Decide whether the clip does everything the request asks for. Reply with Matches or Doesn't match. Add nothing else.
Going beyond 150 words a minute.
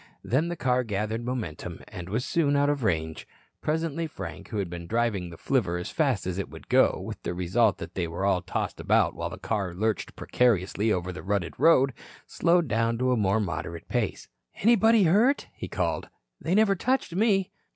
Matches